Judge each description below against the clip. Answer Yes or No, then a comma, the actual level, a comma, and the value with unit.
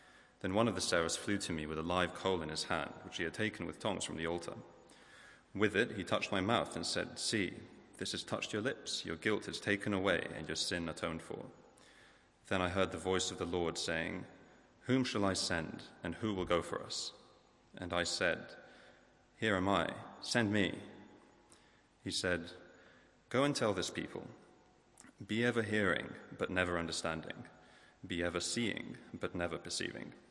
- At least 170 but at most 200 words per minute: Yes, average, 185 wpm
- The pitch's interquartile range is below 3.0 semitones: Yes, narrow, 2.6 semitones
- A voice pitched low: Yes, very low, 90 Hz